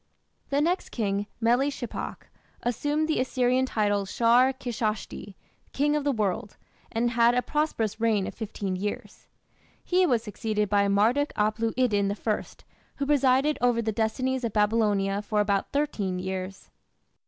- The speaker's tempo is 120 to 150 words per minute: Yes, average, 145 wpm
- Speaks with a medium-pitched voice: No, high, 230 Hz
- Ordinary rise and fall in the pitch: Yes, average, 4.0 semitones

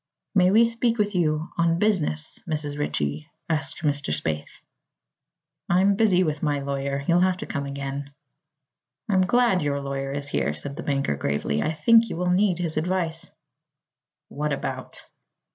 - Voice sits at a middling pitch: Yes, medium, 155 Hz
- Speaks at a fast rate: No, average, 160 wpm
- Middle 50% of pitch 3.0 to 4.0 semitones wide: No, average, 4.7 semitones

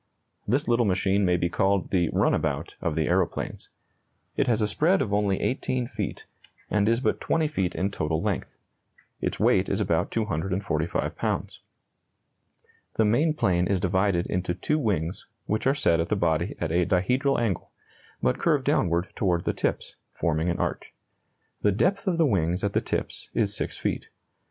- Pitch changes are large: No, average, 4.7 semitones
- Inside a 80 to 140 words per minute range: No, average, 175 wpm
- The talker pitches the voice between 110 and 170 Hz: No, very low, 95 Hz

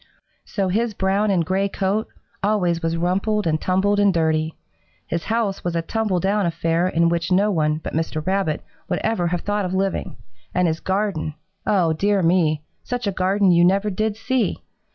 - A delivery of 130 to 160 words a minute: No, average, 185 wpm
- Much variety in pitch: No, average, 3.5 semitones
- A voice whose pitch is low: No, medium, 185 Hz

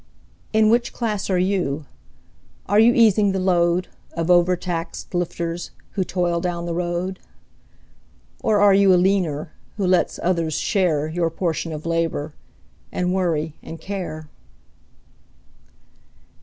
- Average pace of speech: No, slow, 130 wpm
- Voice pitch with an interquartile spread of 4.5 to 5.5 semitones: No, narrow, 2.4 semitones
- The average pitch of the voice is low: No, medium, 175 Hz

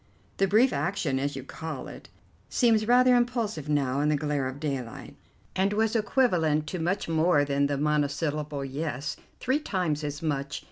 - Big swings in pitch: Yes, wide, 5.8 semitones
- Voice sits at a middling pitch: Yes, medium, 150 Hz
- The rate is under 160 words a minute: No, average, 170 wpm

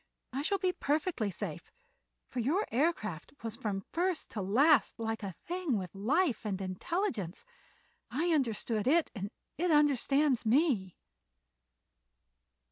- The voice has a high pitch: Yes, very high, 260 Hz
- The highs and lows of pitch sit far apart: Yes, wide, 7.6 semitones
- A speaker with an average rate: No, slow, 125 wpm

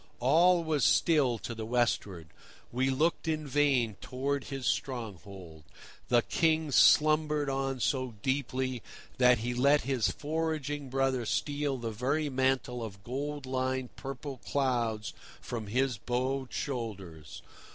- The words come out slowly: Yes, slow, 130 wpm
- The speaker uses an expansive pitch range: No, average, 3.2 semitones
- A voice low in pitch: Yes, low, 130 Hz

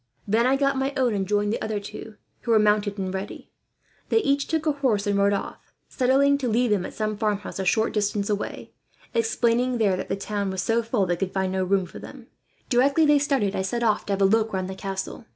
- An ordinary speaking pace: No, fast, 245 wpm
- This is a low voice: No, high, 215 Hz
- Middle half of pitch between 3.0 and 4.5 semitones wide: Yes, average, 4.2 semitones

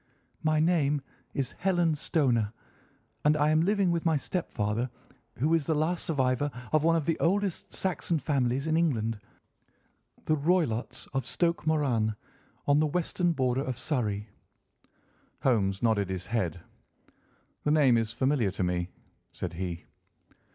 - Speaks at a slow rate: No, average, 145 wpm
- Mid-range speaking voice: Yes, medium, 145 Hz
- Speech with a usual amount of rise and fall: No, wide, 6.0 semitones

